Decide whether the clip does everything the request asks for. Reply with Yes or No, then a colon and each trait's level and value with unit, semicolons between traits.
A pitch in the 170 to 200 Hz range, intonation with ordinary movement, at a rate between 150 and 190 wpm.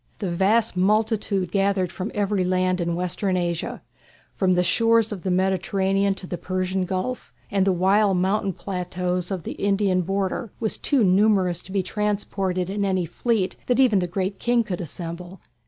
No: high, 190 Hz; narrow, 2.0 semitones; average, 170 wpm